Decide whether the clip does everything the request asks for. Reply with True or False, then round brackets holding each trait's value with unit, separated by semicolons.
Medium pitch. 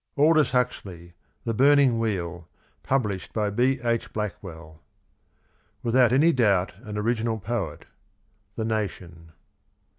False (110 Hz)